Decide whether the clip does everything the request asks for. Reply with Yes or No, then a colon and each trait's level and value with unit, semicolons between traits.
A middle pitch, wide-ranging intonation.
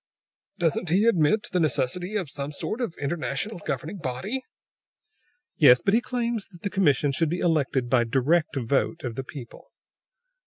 Yes: medium, 160 Hz; wide, 6.0 semitones